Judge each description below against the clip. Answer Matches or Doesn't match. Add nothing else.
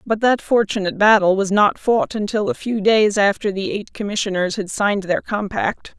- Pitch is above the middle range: Matches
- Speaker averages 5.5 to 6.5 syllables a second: Doesn't match